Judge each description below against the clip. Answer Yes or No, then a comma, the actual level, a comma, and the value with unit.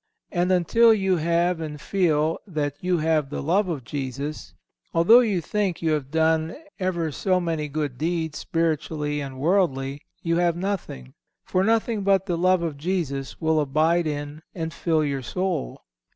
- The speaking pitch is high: No, medium, 165 Hz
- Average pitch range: Yes, average, 3.6 semitones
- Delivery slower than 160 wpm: No, average, 165 wpm